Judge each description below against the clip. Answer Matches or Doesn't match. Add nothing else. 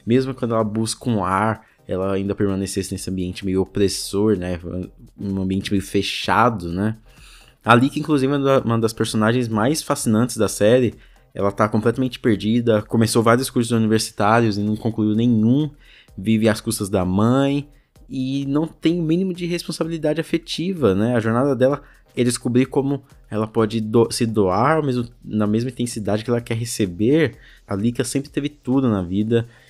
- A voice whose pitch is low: Matches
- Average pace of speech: Matches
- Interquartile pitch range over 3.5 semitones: Matches